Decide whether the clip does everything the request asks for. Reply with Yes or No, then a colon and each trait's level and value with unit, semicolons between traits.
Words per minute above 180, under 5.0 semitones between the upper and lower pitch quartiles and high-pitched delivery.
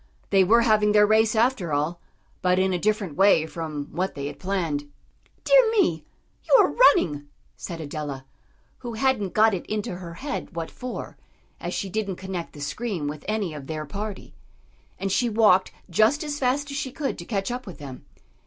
No: average, 190 wpm; wide, 5.6 semitones; high, 195 Hz